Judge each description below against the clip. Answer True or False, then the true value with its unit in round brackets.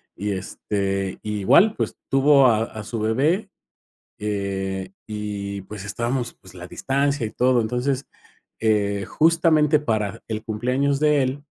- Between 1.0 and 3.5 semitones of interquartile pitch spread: False (5.3 semitones)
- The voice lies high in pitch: False (110 Hz)